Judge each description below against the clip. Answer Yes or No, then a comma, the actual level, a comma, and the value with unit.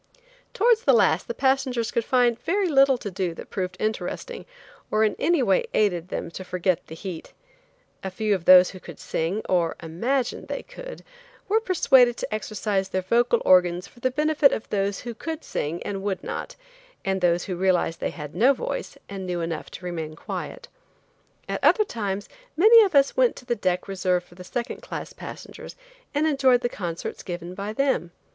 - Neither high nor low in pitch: No, high, 205 Hz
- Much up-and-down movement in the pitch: Yes, wide, 6.7 semitones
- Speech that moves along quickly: No, average, 190 wpm